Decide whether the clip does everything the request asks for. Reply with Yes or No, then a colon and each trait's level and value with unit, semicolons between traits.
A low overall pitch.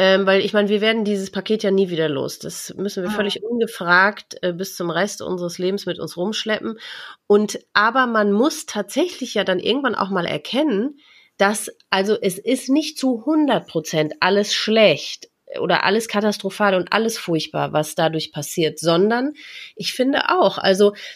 No: high, 205 Hz